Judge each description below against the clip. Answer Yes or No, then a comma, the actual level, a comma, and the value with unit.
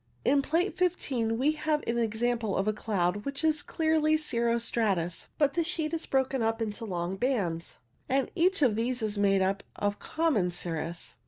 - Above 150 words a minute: Yes, average, 180 wpm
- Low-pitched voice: No, high, 235 Hz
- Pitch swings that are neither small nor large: No, wide, 6.8 semitones